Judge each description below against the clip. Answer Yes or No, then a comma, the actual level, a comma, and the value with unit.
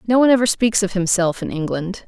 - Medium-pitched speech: No, high, 200 Hz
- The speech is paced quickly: Yes, fast, 230 wpm